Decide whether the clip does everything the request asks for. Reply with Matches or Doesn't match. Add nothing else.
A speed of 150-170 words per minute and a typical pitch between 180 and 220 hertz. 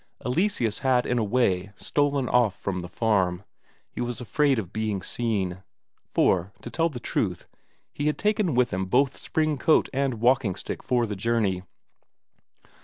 Doesn't match